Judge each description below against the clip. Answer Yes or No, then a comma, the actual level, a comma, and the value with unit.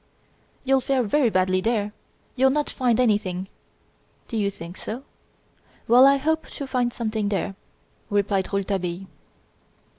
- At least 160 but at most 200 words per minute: No, average, 140 wpm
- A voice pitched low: No, high, 220 Hz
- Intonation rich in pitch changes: No, average, 4.8 semitones